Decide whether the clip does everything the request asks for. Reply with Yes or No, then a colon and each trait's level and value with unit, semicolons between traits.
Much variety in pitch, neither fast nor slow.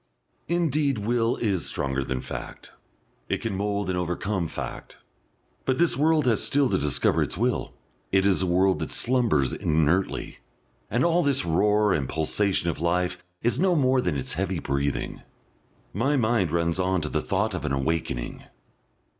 Yes: wide, 6.7 semitones; average, 165 wpm